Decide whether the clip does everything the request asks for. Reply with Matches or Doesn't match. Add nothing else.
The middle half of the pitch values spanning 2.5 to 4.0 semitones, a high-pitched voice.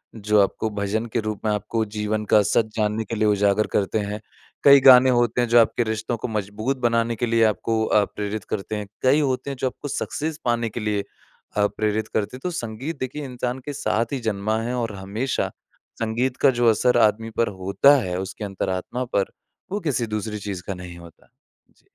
Doesn't match